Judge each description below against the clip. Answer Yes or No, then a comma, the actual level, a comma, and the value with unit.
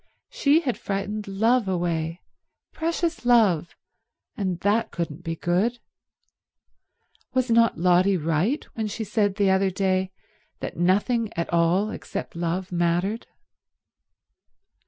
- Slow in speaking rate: Yes, slow, 115 wpm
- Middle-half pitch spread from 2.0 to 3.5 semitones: No, average, 4.5 semitones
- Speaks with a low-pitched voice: No, high, 195 Hz